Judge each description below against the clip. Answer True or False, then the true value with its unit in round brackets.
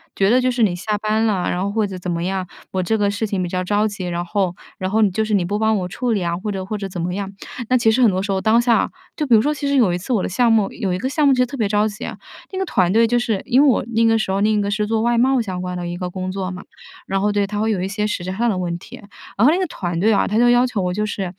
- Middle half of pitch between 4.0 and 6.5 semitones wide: False (3.4 semitones)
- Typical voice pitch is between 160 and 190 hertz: False (205 Hz)